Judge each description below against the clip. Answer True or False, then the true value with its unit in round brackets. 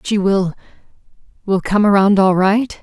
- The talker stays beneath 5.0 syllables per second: True (4.4 syllables/s)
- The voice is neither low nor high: False (195 Hz)